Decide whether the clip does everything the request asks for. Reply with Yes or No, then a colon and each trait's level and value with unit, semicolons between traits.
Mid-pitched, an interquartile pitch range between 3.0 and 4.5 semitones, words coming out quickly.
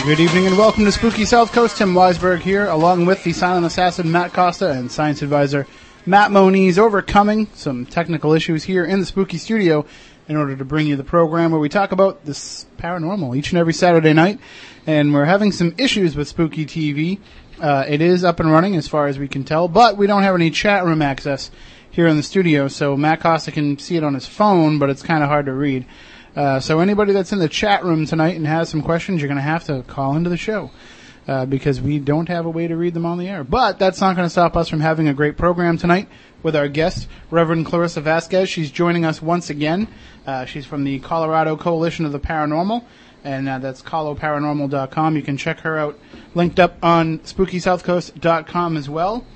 Yes: medium, 165 Hz; average, 3.4 semitones; fast, 220 wpm